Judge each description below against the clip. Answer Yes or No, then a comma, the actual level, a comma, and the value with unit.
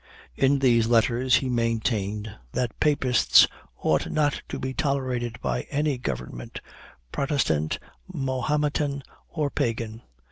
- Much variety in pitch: No, average, 3.8 semitones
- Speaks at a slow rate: Yes, slow, 110 wpm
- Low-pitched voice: Yes, low, 125 Hz